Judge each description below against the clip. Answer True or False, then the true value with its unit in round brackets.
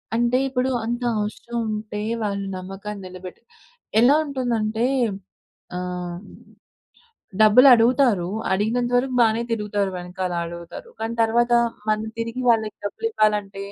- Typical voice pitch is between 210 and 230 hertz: True (215 Hz)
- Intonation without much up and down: False (3.4 semitones)